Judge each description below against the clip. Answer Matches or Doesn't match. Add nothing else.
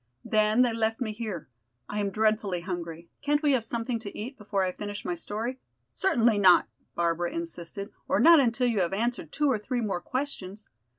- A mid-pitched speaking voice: Doesn't match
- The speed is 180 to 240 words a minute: Matches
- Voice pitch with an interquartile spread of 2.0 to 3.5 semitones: Doesn't match